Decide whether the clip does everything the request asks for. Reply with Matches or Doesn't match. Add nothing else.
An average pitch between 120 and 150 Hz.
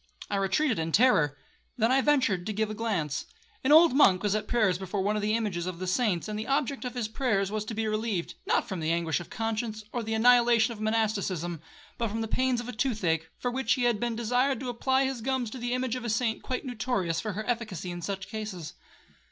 Doesn't match